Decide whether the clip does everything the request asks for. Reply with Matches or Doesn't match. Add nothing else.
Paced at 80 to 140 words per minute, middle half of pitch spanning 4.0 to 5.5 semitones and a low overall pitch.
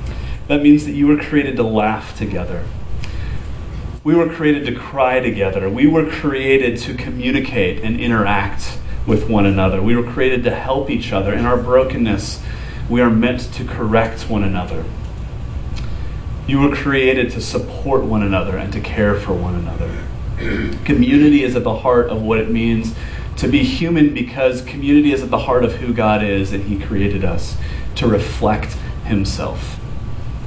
Doesn't match